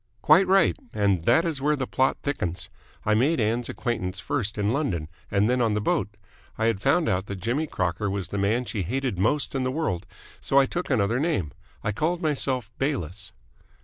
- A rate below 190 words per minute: No, average, 200 wpm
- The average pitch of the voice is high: No, low, 120 Hz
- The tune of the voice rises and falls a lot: Yes, wide, 6.0 semitones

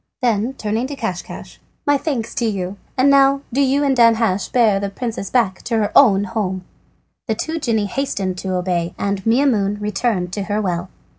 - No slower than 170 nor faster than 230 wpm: Yes, average, 180 wpm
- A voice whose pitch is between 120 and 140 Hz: No, high, 215 Hz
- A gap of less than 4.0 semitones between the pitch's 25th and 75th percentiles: No, average, 4.6 semitones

